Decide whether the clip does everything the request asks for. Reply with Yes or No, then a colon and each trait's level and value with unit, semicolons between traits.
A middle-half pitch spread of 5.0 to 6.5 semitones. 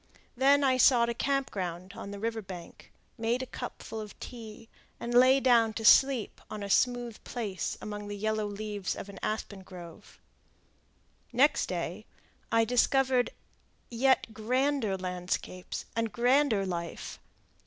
No: average, 3.7 semitones